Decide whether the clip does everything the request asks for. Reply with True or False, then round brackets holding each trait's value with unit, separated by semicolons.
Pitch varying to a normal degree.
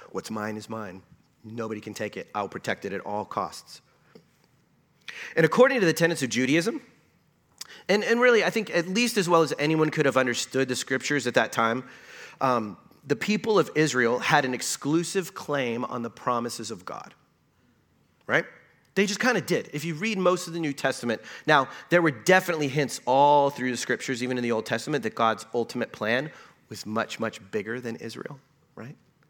False (6.7 semitones)